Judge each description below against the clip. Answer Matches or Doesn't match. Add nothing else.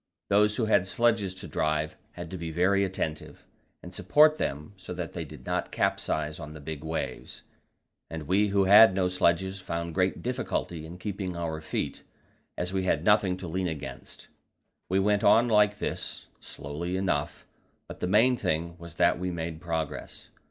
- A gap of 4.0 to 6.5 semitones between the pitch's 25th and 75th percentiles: Doesn't match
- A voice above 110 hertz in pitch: Doesn't match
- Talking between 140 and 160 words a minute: Doesn't match